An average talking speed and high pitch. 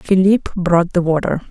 No: average, 160 wpm; medium, 180 Hz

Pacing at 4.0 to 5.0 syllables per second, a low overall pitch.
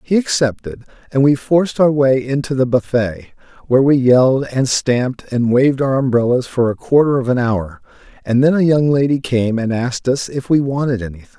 No: 5.4 syllables/s; low, 130 Hz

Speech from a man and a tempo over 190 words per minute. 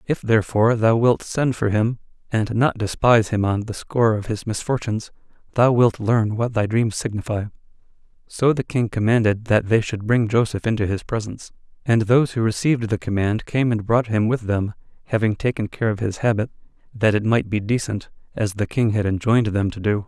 Yes: male; average, 200 wpm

